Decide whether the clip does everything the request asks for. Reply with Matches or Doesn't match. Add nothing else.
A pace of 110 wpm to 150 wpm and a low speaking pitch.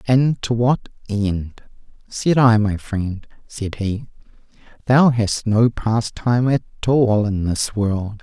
Matches